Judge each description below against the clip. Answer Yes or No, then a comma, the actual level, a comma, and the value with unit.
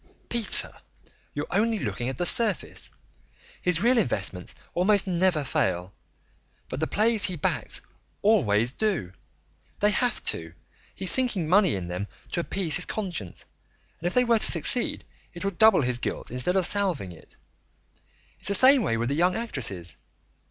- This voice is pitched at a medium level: Yes, medium, 180 Hz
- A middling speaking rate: Yes, average, 160 wpm